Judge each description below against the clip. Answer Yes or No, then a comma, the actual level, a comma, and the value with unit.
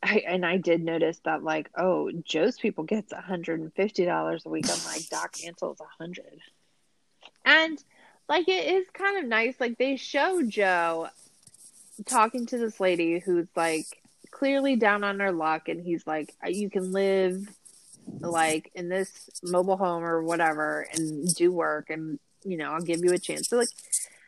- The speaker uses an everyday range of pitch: Yes, average, 4.8 semitones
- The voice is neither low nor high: Yes, medium, 180 Hz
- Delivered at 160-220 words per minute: Yes, average, 165 wpm